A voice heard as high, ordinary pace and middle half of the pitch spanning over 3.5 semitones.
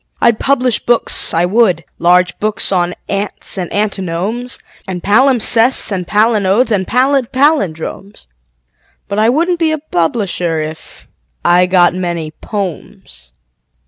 No: high, 200 Hz; slow, 125 wpm; average, 5.2 semitones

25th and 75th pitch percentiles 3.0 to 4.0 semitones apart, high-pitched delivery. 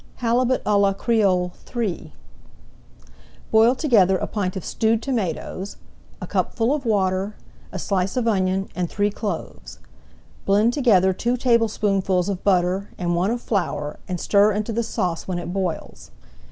Yes: average, 3.6 semitones; high, 200 Hz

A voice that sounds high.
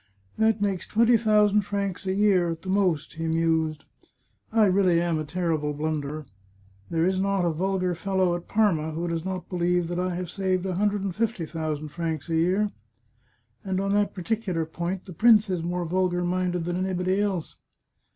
No: medium, 180 Hz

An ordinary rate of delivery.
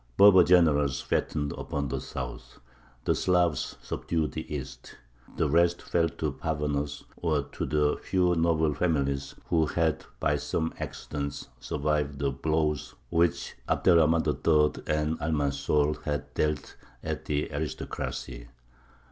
No: slow, 130 wpm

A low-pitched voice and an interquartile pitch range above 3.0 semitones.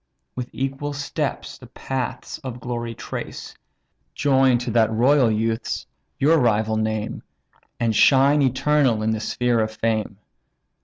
Yes: low, 120 Hz; average, 3.4 semitones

